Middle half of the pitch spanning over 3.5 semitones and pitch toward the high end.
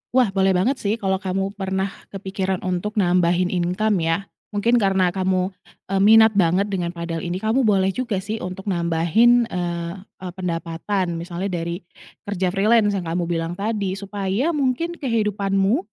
No: average, 2.9 semitones; high, 195 Hz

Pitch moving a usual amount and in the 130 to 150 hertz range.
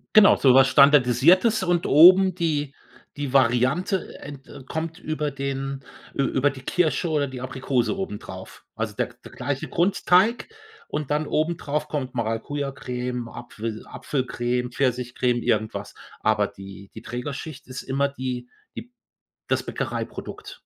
Yes: average, 3.8 semitones; low, 135 Hz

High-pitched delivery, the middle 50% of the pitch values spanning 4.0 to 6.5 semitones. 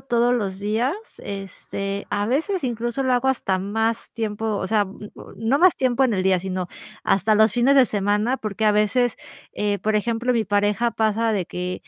No: high, 220 Hz; average, 3.0 semitones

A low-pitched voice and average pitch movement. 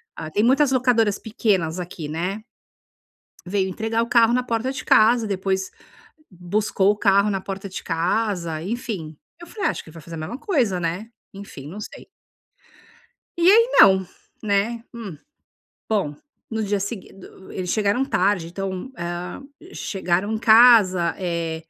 No: high, 200 Hz; average, 4.1 semitones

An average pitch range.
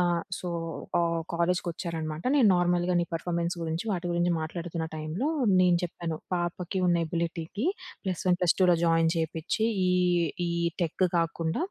No: narrow, 1.4 semitones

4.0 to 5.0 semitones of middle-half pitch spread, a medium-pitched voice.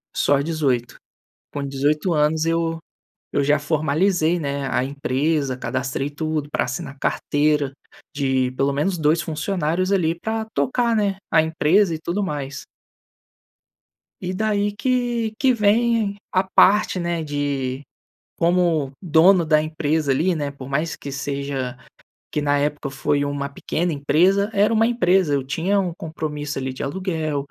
Yes: average, 4.5 semitones; medium, 155 Hz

